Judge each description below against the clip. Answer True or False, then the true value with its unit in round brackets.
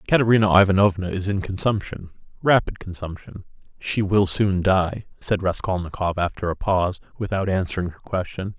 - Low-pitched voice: True (95 Hz)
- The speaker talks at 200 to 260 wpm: False (140 wpm)